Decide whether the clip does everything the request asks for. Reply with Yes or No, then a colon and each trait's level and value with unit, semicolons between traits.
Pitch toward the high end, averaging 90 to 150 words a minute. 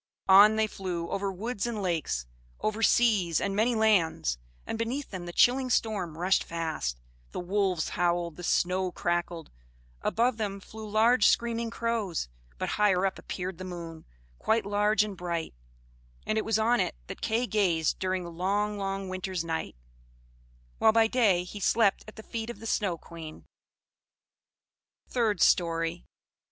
No: high, 195 Hz; average, 160 wpm